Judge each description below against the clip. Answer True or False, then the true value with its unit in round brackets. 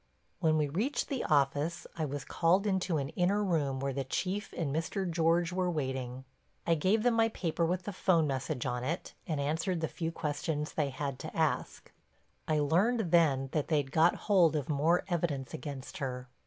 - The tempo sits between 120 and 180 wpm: False (190 wpm)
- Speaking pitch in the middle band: True (160 Hz)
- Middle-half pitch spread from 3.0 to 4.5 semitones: True (4.1 semitones)